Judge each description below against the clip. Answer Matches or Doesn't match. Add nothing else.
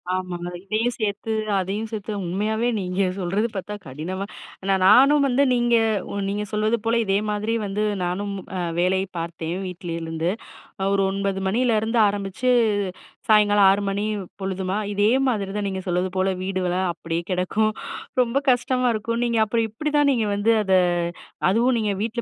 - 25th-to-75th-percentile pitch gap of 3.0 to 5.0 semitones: Matches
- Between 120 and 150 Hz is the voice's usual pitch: Doesn't match